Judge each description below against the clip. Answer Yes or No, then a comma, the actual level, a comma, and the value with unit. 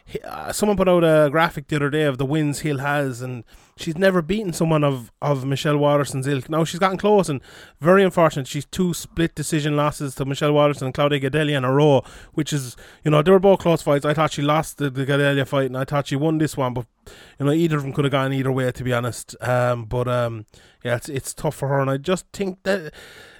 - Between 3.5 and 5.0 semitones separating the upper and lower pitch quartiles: No, average, 2.9 semitones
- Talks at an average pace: No, fast, 245 wpm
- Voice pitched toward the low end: No, medium, 145 Hz